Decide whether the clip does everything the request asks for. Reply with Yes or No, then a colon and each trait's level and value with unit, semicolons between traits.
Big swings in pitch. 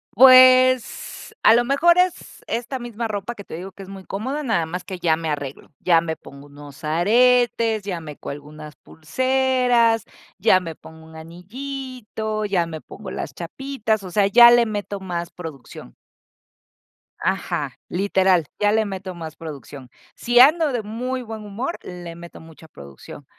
Yes: wide, 6.5 semitones